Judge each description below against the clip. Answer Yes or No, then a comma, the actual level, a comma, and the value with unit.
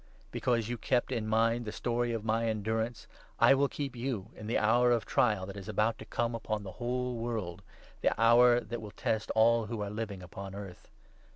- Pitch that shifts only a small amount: Yes, narrow, 2.2 semitones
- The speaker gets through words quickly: Yes, fast, 210 wpm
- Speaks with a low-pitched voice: Yes, low, 115 Hz